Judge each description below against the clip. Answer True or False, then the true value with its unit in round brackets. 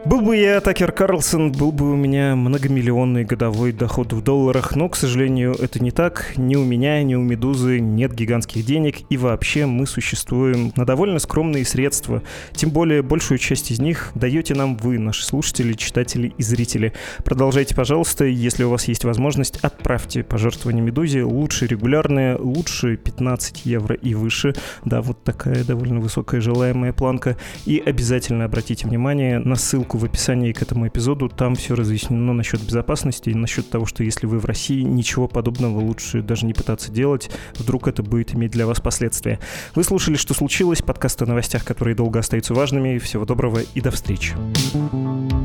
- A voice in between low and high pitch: False (125 Hz)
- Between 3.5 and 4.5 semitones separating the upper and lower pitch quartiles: False (2.9 semitones)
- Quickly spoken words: True (170 wpm)